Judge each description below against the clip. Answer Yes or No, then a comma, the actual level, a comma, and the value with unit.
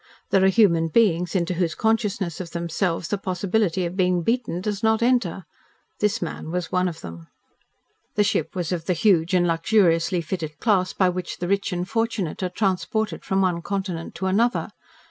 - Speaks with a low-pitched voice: No, medium, 185 Hz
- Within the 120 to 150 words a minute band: No, average, 185 wpm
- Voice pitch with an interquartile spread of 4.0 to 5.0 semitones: No, average, 3.1 semitones